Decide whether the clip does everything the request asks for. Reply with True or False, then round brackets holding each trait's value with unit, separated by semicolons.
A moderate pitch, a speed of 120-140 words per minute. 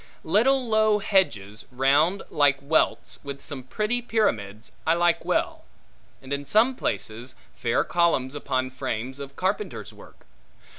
True (145 Hz; 135 wpm)